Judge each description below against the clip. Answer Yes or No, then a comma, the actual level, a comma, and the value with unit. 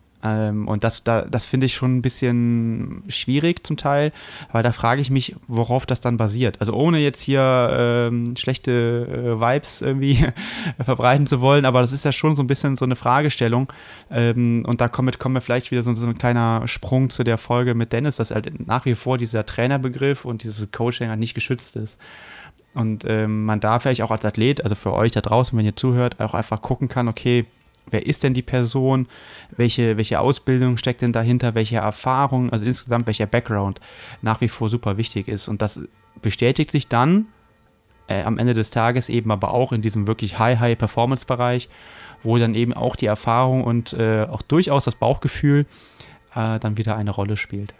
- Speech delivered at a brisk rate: Yes, fast, 195 wpm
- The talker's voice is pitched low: Yes, low, 120 Hz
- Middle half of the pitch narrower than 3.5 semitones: Yes, narrow, 2.6 semitones